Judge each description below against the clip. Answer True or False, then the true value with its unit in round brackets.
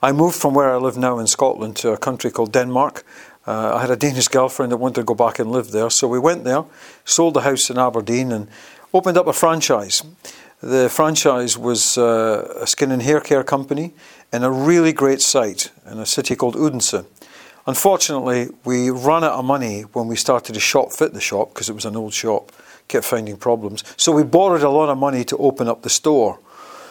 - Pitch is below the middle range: True (130 Hz)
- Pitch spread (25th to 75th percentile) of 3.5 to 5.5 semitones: True (3.9 semitones)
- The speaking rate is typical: False (215 wpm)